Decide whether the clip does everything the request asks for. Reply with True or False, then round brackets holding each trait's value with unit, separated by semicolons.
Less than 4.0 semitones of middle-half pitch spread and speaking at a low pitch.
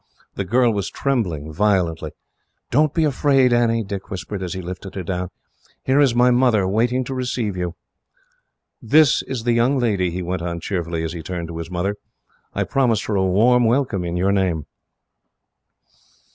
False (5.6 semitones; 100 Hz)